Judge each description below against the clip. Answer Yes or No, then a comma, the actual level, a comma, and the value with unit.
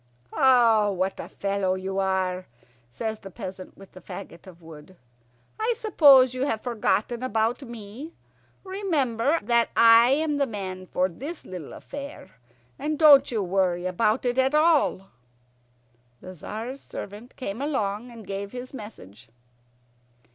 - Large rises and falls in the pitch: Yes, wide, 5.8 semitones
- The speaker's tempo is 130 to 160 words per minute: Yes, average, 140 wpm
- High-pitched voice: Yes, high, 225 Hz